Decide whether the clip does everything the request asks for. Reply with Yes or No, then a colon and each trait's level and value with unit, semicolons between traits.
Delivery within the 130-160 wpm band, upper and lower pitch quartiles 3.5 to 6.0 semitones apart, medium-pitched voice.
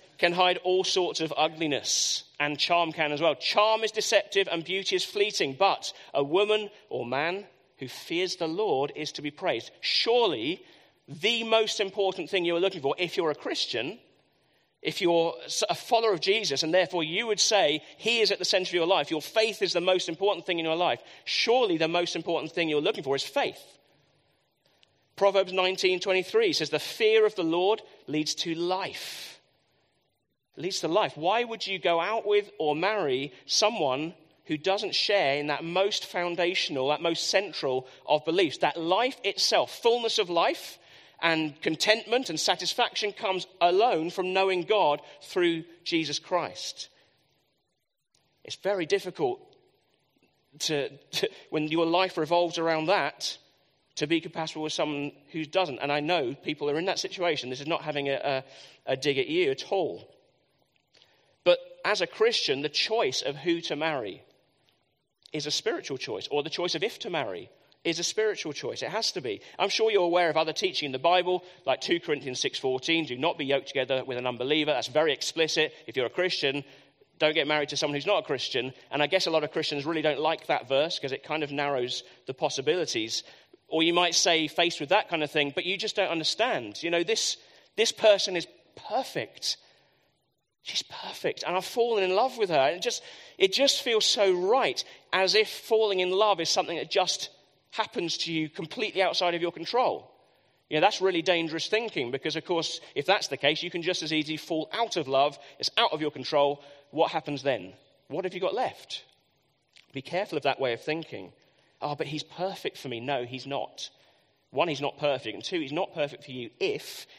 No: average, 195 wpm; average, 4.9 semitones; medium, 175 Hz